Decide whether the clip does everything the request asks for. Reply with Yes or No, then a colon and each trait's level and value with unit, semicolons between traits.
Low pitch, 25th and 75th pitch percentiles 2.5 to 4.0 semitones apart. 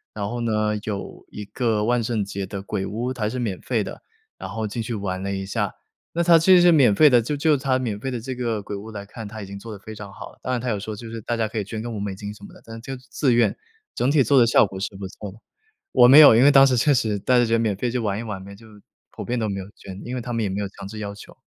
Yes: low, 110 Hz; average, 3.4 semitones